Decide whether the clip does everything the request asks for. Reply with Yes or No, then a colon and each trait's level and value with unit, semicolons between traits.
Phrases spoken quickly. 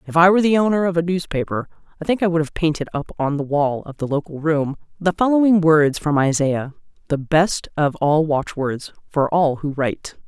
Yes: fast, 210 wpm